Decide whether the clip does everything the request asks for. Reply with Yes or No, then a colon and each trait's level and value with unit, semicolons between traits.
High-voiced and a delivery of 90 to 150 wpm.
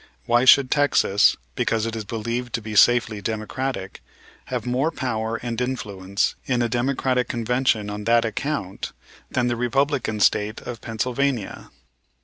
No: low, 120 Hz; average, 140 wpm